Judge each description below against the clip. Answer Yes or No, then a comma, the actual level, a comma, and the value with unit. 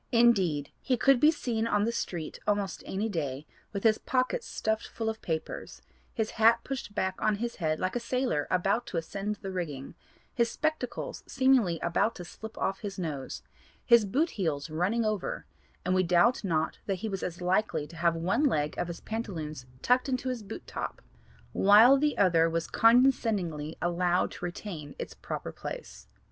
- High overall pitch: Yes, high, 200 Hz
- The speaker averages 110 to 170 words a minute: No, average, 180 wpm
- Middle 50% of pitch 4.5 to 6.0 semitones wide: Yes, wide, 5.6 semitones